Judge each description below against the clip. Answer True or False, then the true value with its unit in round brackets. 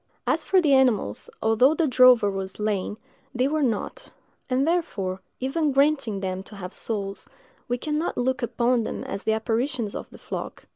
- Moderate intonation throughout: True (4.9 semitones)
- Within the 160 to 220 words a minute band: True (180 wpm)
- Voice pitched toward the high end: True (245 Hz)